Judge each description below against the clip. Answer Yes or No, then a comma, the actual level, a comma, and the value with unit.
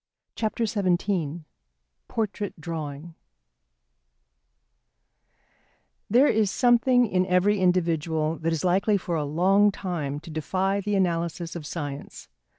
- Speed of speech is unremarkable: No, slow, 105 wpm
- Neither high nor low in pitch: Yes, medium, 180 Hz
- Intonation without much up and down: No, average, 3.8 semitones